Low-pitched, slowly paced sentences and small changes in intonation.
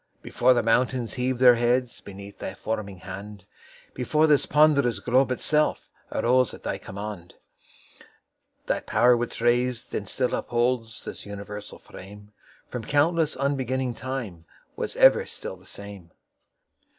No: low, 120 Hz; slow, 110 wpm; average, 4.0 semitones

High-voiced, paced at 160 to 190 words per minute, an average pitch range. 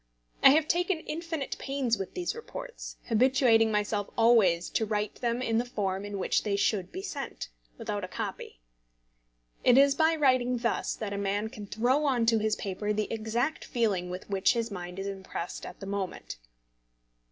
Yes: high, 225 Hz; average, 180 wpm; average, 4.8 semitones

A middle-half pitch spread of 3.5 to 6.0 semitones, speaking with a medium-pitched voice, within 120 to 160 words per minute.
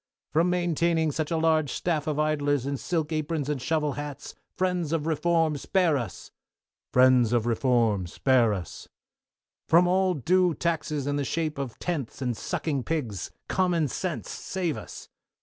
Yes: average, 3.8 semitones; medium, 155 Hz; average, 155 wpm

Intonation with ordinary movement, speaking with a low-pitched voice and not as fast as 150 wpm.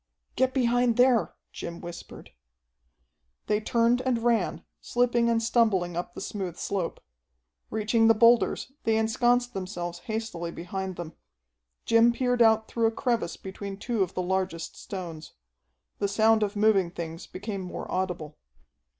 No: average, 4.3 semitones; high, 215 Hz; average, 140 wpm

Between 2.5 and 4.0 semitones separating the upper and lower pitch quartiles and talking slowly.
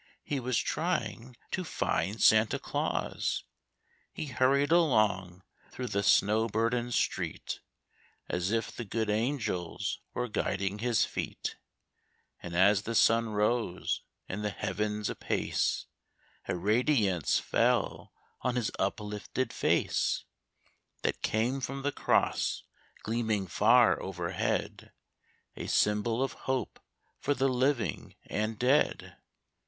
Yes: average, 3.5 semitones; slow, 115 wpm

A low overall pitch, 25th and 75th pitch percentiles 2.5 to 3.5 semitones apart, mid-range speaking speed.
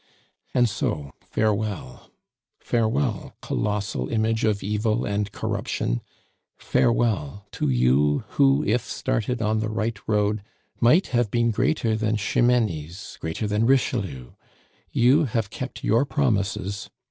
No: low, 110 Hz; average, 2.9 semitones; slow, 120 wpm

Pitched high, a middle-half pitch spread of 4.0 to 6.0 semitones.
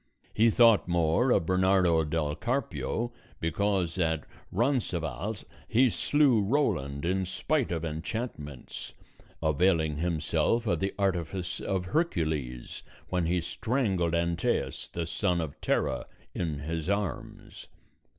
No: very low, 90 Hz; average, 4.7 semitones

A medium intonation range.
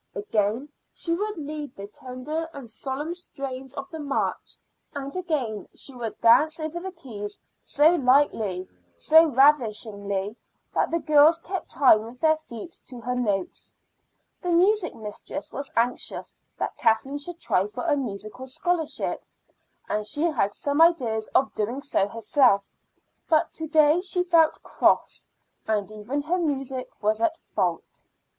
No: wide, 6.3 semitones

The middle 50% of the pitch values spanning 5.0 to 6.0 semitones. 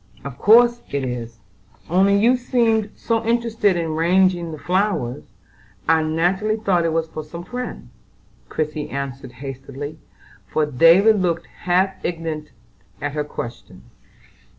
Yes: wide, 5.4 semitones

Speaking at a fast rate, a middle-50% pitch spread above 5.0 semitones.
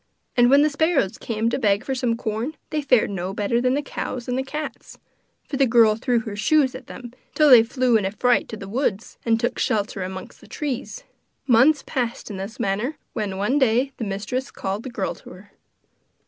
No: fast, 215 wpm; average, 4.0 semitones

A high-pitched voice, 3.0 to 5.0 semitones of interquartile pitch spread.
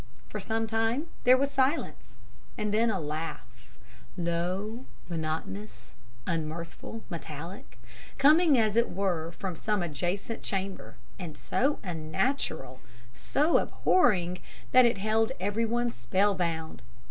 No: high, 195 Hz; wide, 5.6 semitones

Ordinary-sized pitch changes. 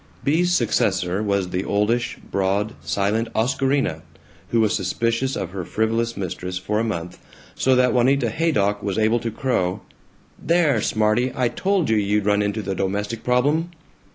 Yes: average, 3.9 semitones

